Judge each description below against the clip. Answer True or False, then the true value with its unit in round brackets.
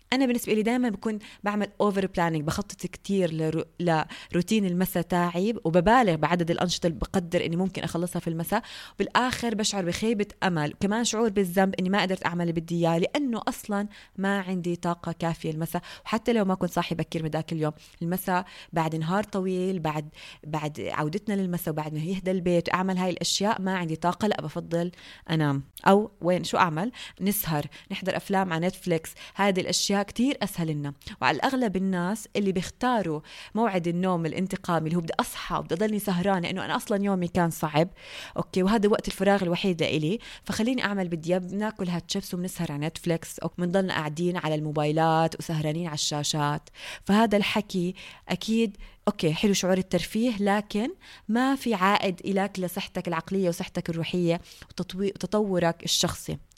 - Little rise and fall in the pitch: False (3.4 semitones)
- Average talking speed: False (160 wpm)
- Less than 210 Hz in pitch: True (185 Hz)